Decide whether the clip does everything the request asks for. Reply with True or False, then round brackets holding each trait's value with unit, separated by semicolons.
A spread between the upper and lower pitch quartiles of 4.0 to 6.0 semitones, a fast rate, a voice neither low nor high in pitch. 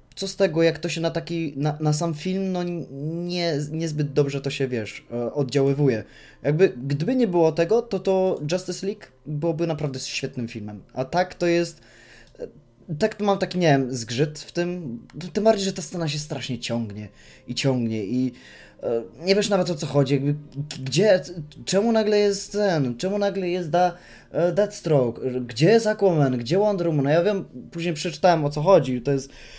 True (5.2 semitones; 185 wpm; 160 Hz)